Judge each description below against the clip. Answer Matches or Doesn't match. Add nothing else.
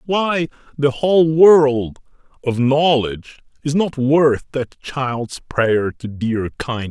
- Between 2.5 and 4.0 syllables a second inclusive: Matches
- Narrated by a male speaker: Matches